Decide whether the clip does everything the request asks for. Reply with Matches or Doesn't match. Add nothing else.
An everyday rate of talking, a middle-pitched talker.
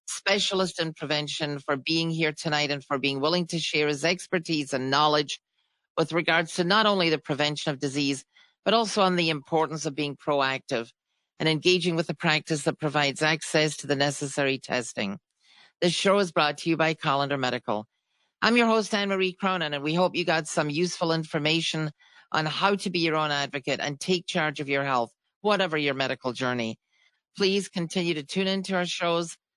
Matches